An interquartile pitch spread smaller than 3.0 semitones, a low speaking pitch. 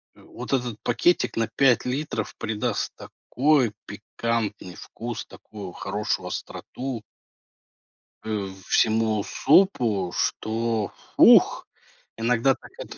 Yes: narrow, 2.6 semitones; low, 115 Hz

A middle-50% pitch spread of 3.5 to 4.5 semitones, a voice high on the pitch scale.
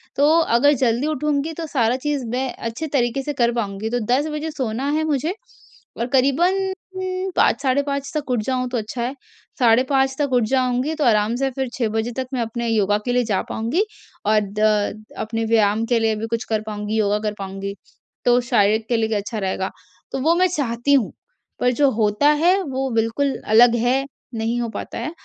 Yes: average, 3.9 semitones; high, 245 Hz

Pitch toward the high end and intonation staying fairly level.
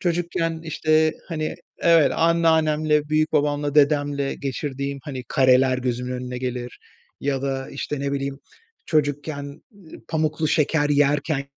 No: medium, 145 Hz; narrow, 2.2 semitones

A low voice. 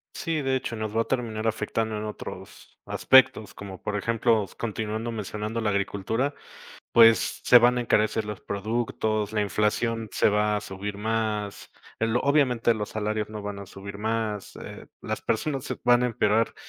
Yes: low, 110 Hz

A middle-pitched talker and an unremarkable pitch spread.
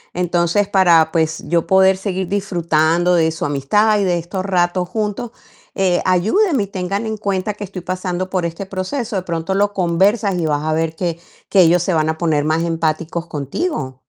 Yes: medium, 180 Hz; average, 3.1 semitones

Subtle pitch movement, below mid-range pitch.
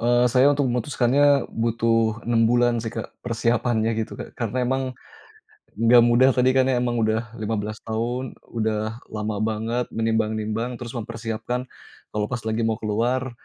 Yes: narrow, 1.8 semitones; low, 115 Hz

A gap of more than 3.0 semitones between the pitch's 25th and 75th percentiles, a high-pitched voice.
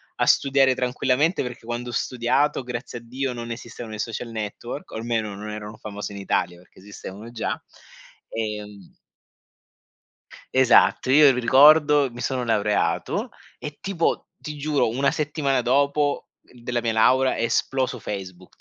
No: average, 3.8 semitones; low, 120 Hz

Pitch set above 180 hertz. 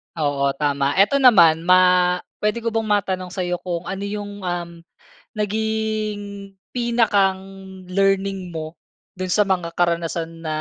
Yes: high, 190 Hz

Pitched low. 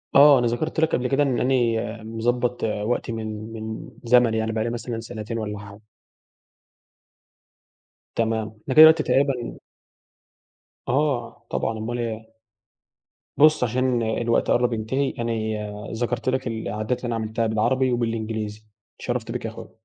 Yes: low, 115 Hz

